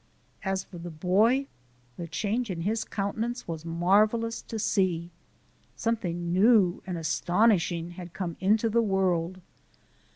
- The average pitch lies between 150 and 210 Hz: Yes, high, 190 Hz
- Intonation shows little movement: No, average, 4.1 semitones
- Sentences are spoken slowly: Yes, slow, 130 wpm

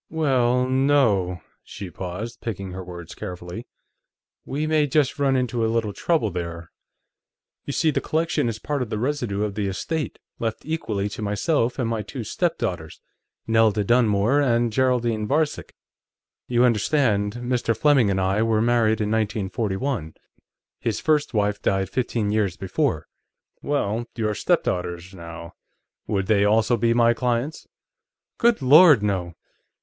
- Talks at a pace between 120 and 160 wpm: Yes, average, 145 wpm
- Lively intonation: No, average, 4.5 semitones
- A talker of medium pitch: No, low, 115 Hz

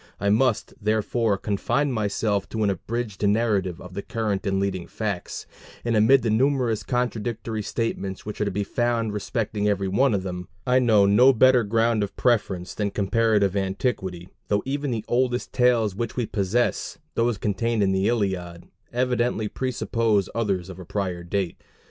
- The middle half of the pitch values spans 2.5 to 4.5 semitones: Yes, average, 3.3 semitones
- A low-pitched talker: Yes, low, 105 Hz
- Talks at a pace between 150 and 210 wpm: Yes, average, 165 wpm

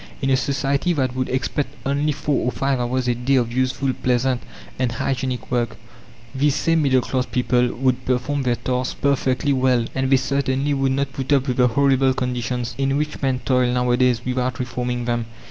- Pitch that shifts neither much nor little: No, narrow, 1.7 semitones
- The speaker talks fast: No, average, 190 wpm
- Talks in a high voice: No, low, 130 Hz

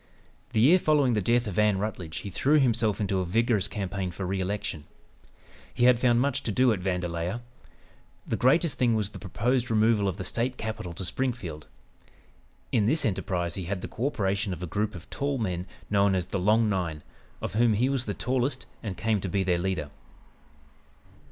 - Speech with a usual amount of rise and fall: Yes, average, 4.5 semitones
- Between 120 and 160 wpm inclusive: No, average, 195 wpm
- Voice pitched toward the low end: Yes, low, 105 Hz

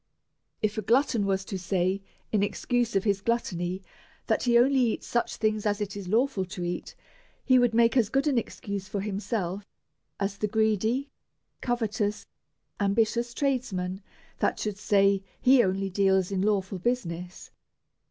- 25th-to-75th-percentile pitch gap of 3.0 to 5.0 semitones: Yes, average, 3.5 semitones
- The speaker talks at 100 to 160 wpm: Yes, average, 155 wpm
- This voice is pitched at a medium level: No, high, 210 Hz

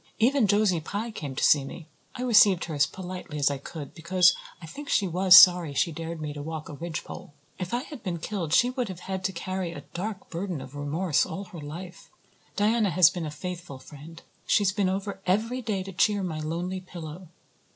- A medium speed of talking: No, fast, 210 wpm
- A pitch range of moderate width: Yes, average, 3.7 semitones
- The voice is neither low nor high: Yes, medium, 180 Hz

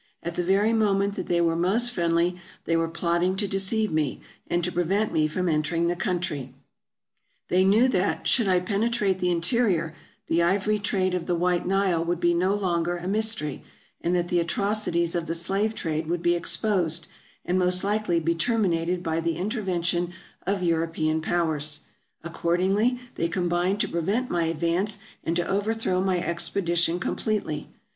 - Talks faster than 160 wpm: Yes, average, 175 wpm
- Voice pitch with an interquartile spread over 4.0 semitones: No, average, 2.8 semitones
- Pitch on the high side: No, medium, 175 Hz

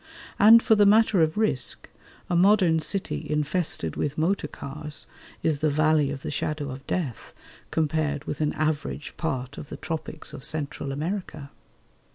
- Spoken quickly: No, average, 160 wpm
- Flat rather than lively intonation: No, average, 3.3 semitones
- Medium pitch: Yes, medium, 155 Hz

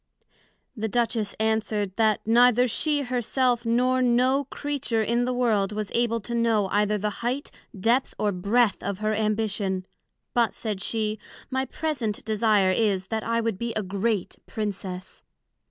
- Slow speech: No, average, 155 wpm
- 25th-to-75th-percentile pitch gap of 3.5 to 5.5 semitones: No, narrow, 2.6 semitones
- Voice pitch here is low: No, high, 220 Hz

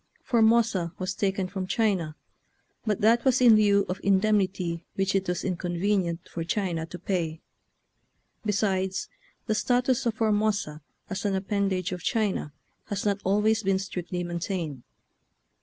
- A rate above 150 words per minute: No, average, 140 wpm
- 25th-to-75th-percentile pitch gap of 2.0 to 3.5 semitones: Yes, average, 3.0 semitones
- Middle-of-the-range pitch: No, high, 195 Hz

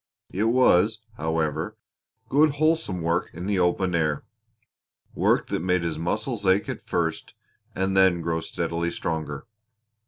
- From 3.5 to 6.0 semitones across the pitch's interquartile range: Yes, average, 4.0 semitones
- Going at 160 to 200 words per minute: No, slow, 135 wpm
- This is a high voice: No, very low, 90 Hz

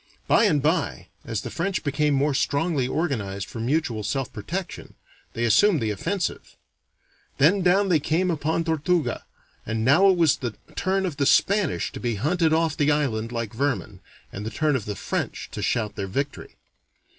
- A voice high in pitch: No, medium, 145 Hz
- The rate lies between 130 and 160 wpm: No, average, 180 wpm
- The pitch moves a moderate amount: No, wide, 6.3 semitones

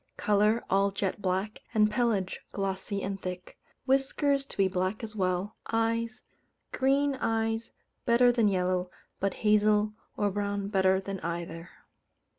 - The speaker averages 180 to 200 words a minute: No, slow, 135 wpm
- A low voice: No, high, 205 Hz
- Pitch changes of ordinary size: Yes, average, 3.0 semitones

